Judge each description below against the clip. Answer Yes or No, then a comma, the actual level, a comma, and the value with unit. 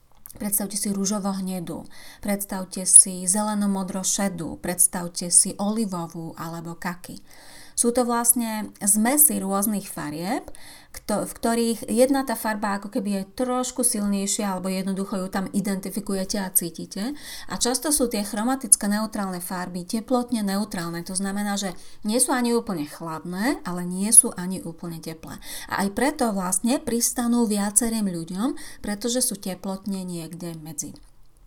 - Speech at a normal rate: Yes, average, 135 wpm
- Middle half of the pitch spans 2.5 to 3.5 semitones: No, average, 4.1 semitones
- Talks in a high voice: Yes, high, 200 Hz